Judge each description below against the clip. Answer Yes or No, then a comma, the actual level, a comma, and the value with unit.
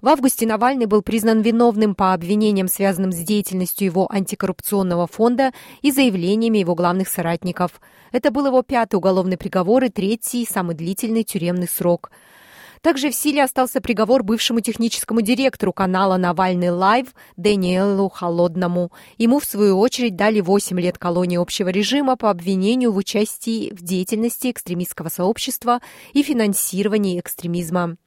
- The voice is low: No, high, 205 Hz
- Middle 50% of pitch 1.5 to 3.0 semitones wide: No, average, 4.2 semitones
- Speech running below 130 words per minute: No, average, 140 wpm